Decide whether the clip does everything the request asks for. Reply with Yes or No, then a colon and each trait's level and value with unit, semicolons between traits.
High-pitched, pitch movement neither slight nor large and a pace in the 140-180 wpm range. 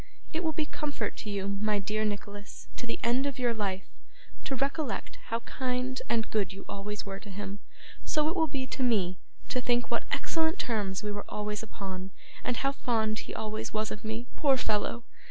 No: high, 220 Hz; average, 4.1 semitones; average, 200 wpm